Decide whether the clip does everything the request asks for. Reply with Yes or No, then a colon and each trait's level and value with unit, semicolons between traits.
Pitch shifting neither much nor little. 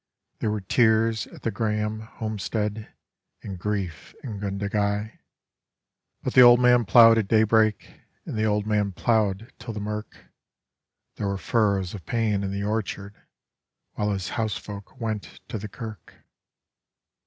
No: narrow, 1.7 semitones